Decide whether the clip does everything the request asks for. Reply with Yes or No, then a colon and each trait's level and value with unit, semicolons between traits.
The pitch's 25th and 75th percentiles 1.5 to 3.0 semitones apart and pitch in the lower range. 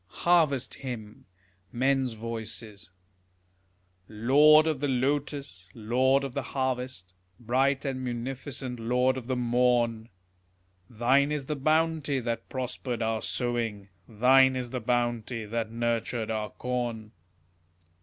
Yes: narrow, 2.6 semitones; low, 125 Hz